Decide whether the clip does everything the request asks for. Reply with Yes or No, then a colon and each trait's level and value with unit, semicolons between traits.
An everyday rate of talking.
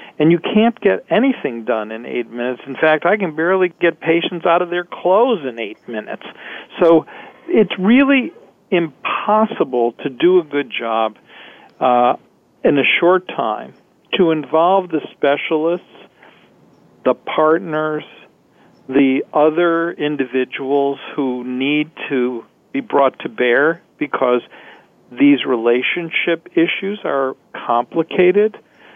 No: slow, 120 wpm